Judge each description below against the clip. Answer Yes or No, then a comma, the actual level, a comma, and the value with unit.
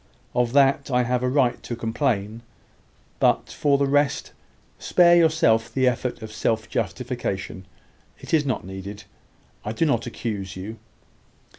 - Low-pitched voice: Yes, low, 120 Hz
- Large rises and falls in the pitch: No, average, 4.1 semitones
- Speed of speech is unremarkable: Yes, average, 145 wpm